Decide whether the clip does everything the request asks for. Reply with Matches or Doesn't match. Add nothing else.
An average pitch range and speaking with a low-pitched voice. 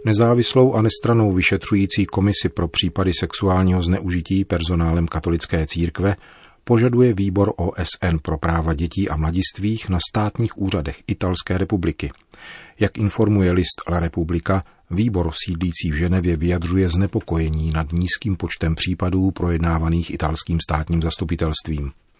Matches